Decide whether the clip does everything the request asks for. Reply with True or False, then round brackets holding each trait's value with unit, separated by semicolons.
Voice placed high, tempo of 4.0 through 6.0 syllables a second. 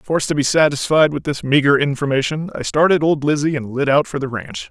False (145 Hz; 5.9 syllables/s)